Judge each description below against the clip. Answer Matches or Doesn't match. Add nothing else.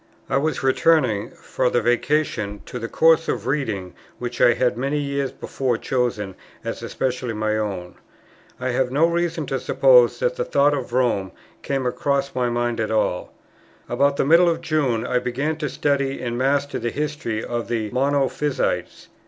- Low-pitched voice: Matches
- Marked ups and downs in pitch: Doesn't match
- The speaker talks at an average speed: Matches